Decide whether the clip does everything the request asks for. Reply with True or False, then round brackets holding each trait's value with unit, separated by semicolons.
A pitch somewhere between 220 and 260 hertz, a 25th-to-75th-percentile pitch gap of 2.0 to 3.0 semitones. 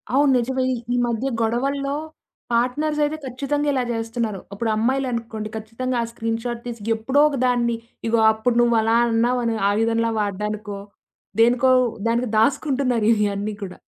True (235 Hz; 2.6 semitones)